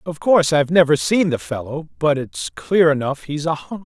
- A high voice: No, medium, 160 Hz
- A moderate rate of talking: No, fast, 215 wpm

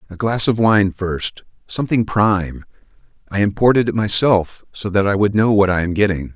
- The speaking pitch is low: Yes, low, 100 Hz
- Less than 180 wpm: Yes, average, 170 wpm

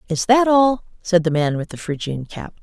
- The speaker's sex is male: No, female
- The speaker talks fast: Yes, fast, 230 wpm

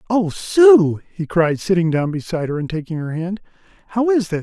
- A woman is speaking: No, male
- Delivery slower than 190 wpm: No, fast, 205 wpm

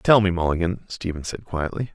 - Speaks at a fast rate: No, average, 185 wpm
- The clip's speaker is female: No, male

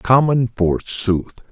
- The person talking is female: No, male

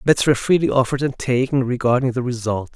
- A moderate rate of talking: Yes, average, 195 wpm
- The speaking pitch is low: Yes, low, 130 Hz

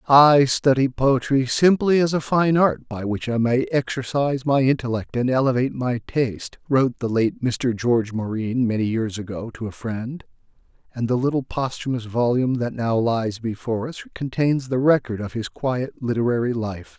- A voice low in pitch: Yes, low, 125 Hz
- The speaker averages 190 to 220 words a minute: No, average, 175 wpm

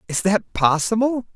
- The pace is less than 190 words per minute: Yes, slow, 135 wpm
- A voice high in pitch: Yes, high, 205 Hz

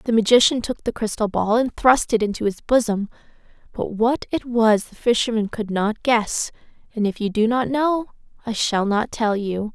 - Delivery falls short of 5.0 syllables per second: Yes, 4.8 syllables/s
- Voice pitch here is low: No, high, 225 Hz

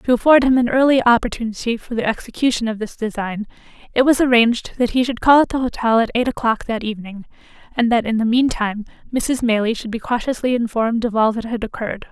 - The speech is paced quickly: Yes, fast, 215 wpm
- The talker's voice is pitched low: No, high, 235 Hz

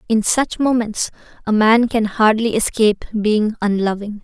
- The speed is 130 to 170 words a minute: Yes, average, 140 wpm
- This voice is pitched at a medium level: No, high, 220 Hz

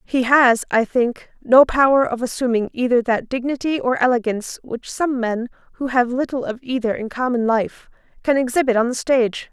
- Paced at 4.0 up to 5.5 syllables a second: Yes, 5.1 syllables/s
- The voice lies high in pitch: Yes, very high, 250 Hz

